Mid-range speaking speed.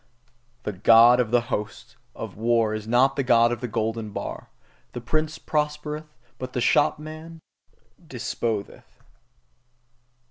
No: slow, 130 wpm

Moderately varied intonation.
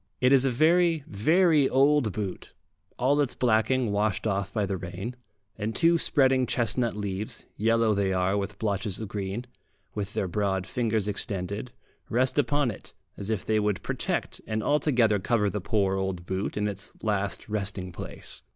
Yes: average, 4.2 semitones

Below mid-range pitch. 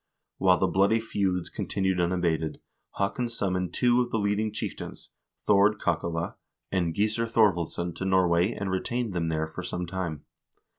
Yes: very low, 95 Hz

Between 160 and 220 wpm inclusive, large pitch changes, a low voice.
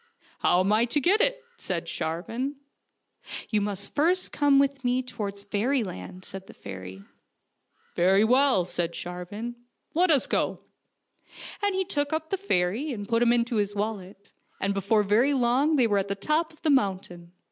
No: average, 195 wpm; wide, 6.4 semitones; high, 225 Hz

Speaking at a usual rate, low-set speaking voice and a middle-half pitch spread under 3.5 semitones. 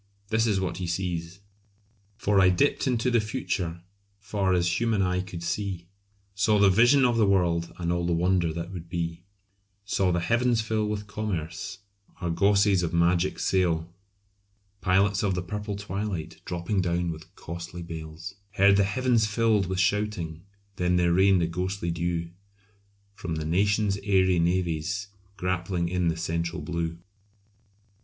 Yes: average, 155 wpm; very low, 90 Hz; average, 3.1 semitones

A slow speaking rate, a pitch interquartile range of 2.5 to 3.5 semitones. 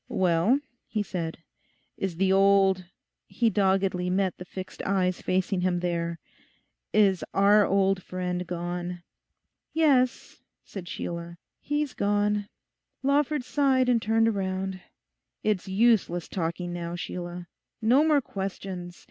Yes: slow, 120 wpm; average, 3.1 semitones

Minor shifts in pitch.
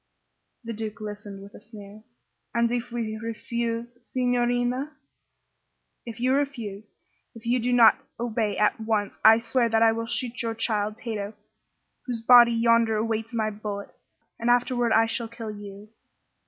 Yes: narrow, 1.9 semitones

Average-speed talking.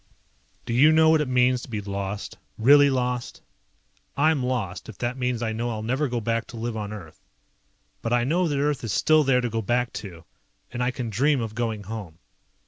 No: fast, 215 wpm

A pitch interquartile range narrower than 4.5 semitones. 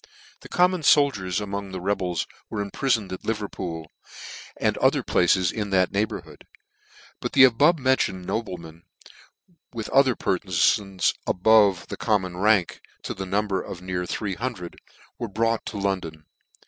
Yes: average, 3.5 semitones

